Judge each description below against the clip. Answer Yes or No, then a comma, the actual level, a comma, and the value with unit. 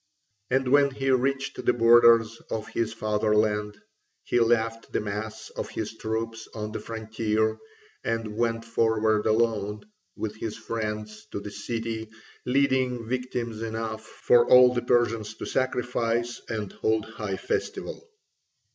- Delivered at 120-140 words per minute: Yes, slow, 135 wpm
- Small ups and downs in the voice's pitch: Yes, narrow, 1.7 semitones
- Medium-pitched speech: No, low, 115 Hz